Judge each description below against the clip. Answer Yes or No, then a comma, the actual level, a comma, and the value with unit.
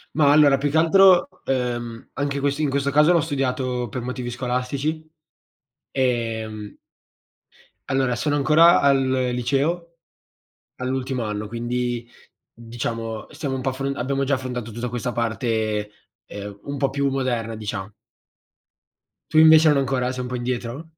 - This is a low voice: Yes, low, 130 Hz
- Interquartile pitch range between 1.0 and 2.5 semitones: No, average, 2.9 semitones